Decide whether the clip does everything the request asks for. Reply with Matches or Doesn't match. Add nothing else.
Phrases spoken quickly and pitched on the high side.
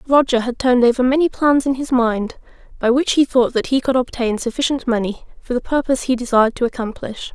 Matches